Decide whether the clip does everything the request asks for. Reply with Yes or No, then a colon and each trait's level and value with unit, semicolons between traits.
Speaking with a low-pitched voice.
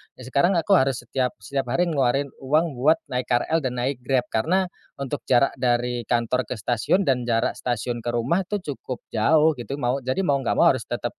Yes: low, 130 Hz